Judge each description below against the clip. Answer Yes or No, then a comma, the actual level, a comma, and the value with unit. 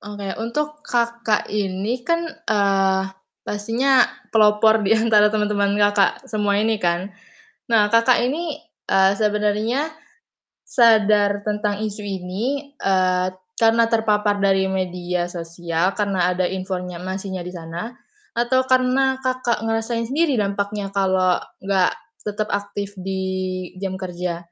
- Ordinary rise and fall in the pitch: Yes, average, 3.2 semitones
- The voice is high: Yes, high, 205 Hz